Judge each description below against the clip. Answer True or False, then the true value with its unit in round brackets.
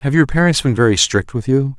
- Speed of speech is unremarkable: False (270 wpm)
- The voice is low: True (130 Hz)